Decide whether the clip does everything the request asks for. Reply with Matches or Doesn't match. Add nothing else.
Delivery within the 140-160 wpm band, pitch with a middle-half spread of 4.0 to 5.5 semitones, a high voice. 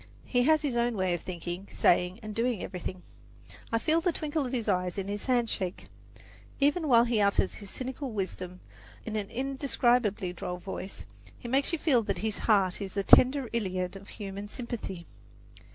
Doesn't match